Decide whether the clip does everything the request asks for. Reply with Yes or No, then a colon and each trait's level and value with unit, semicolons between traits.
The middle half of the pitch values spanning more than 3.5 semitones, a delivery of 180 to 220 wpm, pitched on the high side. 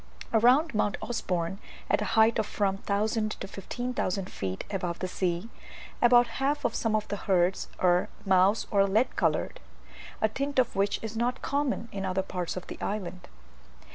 No: average, 3.9 semitones; average, 170 wpm; high, 205 Hz